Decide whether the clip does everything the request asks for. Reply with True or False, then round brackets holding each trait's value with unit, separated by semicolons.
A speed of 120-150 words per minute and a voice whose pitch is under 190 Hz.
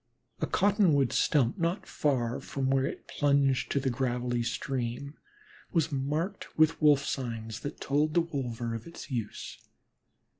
True (145 wpm; 135 Hz)